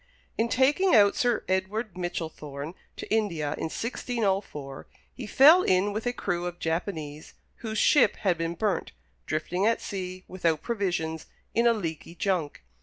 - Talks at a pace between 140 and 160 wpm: Yes, average, 150 wpm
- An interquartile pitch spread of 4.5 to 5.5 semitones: Yes, average, 5.2 semitones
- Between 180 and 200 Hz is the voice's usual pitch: Yes, medium, 185 Hz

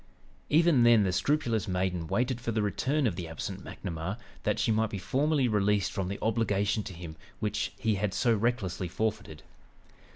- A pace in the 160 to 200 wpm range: Yes, average, 175 wpm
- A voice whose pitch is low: Yes, low, 105 Hz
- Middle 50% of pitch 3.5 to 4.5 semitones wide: Yes, average, 4.1 semitones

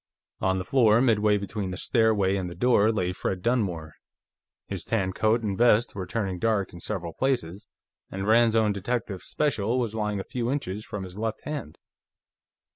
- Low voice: Yes, low, 105 Hz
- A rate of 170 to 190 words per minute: Yes, average, 180 wpm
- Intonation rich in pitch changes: No, average, 3.4 semitones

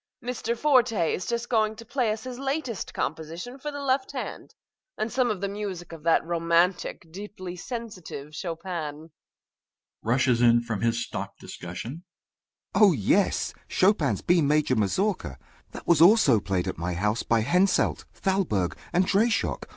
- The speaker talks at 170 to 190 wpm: No, average, 160 wpm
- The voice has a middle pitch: Yes, medium, 175 Hz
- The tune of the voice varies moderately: No, wide, 8.1 semitones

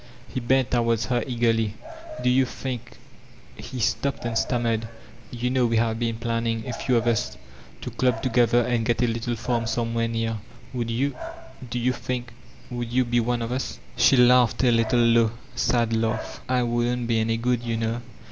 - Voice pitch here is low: Yes, low, 120 Hz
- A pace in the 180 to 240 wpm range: Yes, average, 190 wpm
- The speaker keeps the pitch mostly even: Yes, narrow, 1.3 semitones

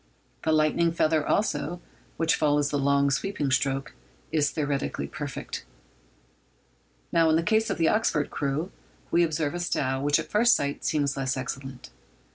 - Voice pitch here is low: No, medium, 150 Hz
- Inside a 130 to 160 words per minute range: Yes, average, 155 wpm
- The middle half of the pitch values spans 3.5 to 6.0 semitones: No, average, 2.9 semitones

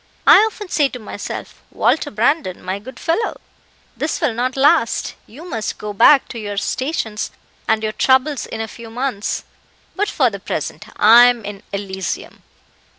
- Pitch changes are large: No, average, 4.6 semitones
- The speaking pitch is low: No, high, 230 Hz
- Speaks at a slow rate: No, average, 165 wpm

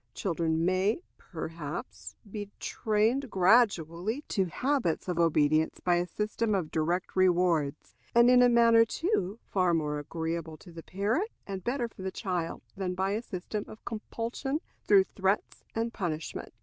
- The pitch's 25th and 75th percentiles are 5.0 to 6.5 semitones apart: Yes, average, 5.3 semitones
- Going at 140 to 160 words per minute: Yes, average, 150 wpm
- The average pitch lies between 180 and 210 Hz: Yes, high, 190 Hz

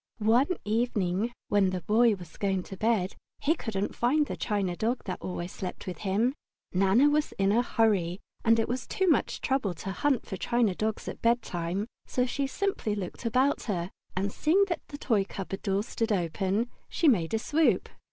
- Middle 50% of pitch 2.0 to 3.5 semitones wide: No, average, 4.4 semitones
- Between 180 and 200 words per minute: Yes, average, 190 wpm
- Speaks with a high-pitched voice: Yes, high, 215 Hz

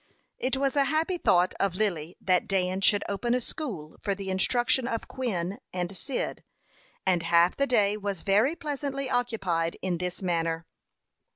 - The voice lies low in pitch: No, high, 200 Hz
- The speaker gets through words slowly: No, average, 165 wpm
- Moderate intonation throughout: No, wide, 5.9 semitones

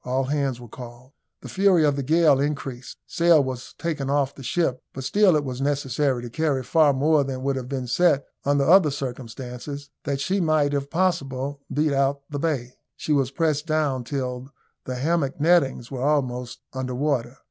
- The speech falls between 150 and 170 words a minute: No, average, 190 wpm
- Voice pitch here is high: No, medium, 140 Hz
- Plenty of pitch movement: No, average, 2.8 semitones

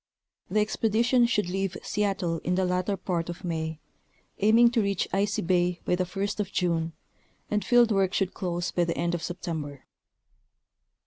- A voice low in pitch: No, medium, 185 Hz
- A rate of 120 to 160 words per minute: No, average, 170 wpm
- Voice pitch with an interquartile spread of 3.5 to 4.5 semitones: No, average, 3.1 semitones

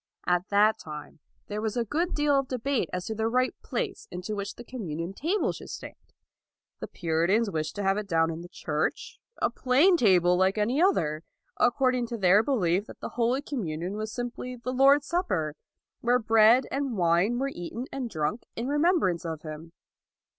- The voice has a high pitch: Yes, high, 220 Hz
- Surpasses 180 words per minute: Yes, average, 190 wpm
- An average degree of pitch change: No, wide, 6.5 semitones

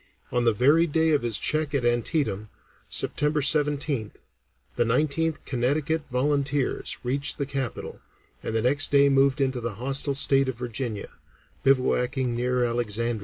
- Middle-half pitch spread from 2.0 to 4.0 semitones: Yes, average, 3.2 semitones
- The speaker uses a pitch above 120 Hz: Yes, low, 135 Hz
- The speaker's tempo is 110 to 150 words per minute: Yes, average, 145 wpm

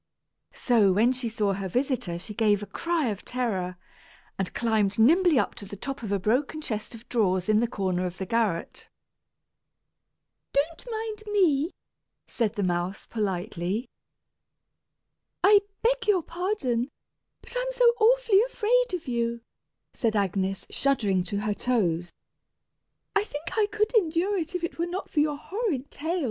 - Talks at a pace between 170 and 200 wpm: No, average, 155 wpm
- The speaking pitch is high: Yes, high, 245 Hz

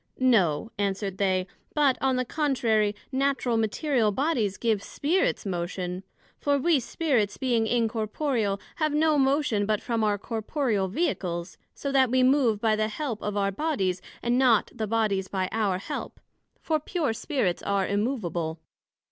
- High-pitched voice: Yes, high, 225 Hz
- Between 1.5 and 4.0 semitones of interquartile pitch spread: No, average, 5.2 semitones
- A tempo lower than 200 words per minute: Yes, average, 150 wpm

